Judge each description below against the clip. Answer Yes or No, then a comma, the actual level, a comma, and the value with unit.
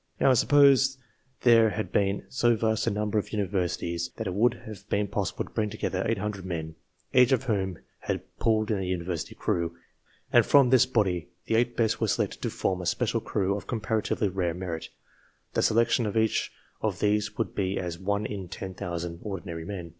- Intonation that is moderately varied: Yes, average, 3.4 semitones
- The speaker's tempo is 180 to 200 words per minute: Yes, average, 190 wpm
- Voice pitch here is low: Yes, low, 105 Hz